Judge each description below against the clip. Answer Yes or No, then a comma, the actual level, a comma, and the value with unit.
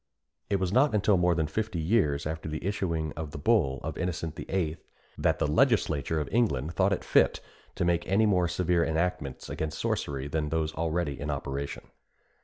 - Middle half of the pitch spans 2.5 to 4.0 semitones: Yes, average, 3.7 semitones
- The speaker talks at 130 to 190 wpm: Yes, average, 180 wpm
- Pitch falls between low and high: No, very low, 80 Hz